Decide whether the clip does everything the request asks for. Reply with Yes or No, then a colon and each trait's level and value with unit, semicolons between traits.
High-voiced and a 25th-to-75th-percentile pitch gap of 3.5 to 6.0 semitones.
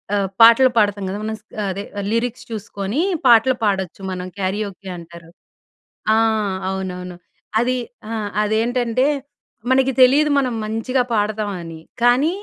Yes: high, 215 Hz; average, 4.2 semitones